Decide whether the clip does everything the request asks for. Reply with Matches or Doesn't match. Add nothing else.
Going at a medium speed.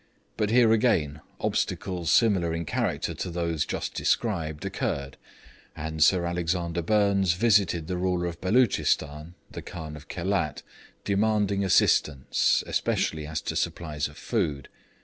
Doesn't match